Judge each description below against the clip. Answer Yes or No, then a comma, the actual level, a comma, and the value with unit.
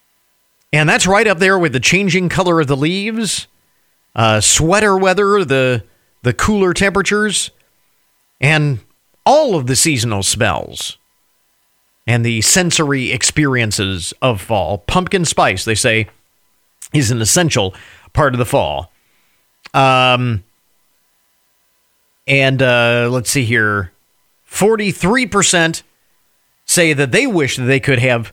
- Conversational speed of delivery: No, slow, 125 wpm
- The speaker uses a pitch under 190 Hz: Yes, low, 135 Hz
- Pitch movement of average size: No, wide, 7.4 semitones